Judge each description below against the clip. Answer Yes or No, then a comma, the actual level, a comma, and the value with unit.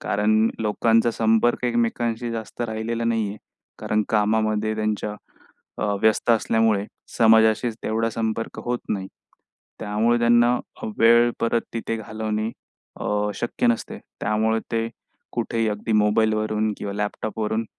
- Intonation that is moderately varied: No, narrow, 1.3 semitones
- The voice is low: Yes, low, 110 Hz